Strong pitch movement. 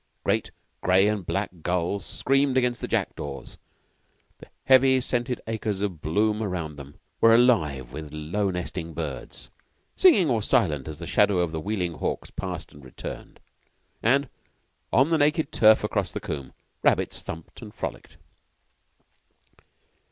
Yes: wide, 7.3 semitones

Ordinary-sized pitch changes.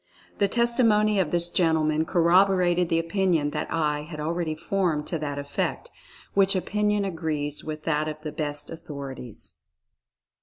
Yes: average, 4.0 semitones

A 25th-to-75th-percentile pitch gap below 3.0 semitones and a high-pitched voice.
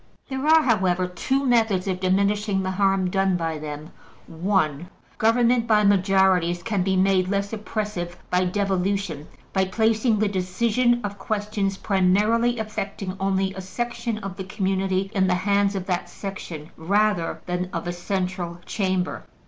Yes: narrow, 2.5 semitones; high, 195 Hz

